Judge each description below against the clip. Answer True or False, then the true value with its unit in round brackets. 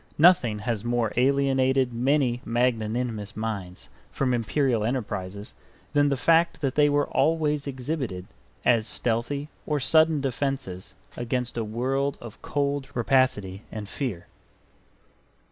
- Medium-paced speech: False (120 wpm)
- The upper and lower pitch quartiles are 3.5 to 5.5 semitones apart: True (4.0 semitones)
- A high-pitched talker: False (125 Hz)